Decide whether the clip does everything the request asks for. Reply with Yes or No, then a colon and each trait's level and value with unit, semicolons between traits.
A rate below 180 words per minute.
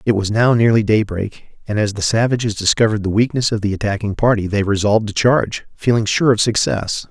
No: fast, 205 wpm